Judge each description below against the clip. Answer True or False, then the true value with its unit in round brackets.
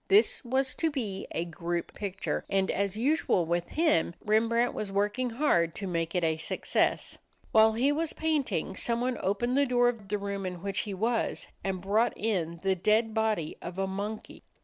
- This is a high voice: True (210 Hz)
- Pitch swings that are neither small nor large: True (4.6 semitones)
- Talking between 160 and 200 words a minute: True (185 wpm)